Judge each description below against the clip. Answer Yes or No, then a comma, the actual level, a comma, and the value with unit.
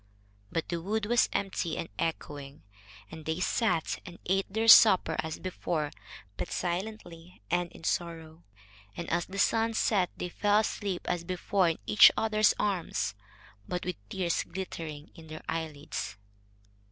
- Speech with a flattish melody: No, average, 3.5 semitones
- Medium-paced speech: Yes, average, 150 wpm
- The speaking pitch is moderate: Yes, medium, 175 Hz